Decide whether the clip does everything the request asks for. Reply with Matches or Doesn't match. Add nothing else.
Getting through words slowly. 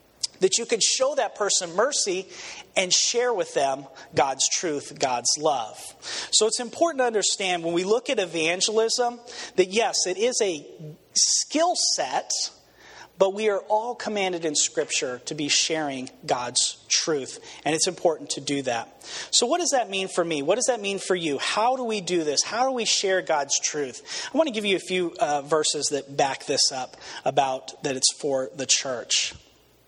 Doesn't match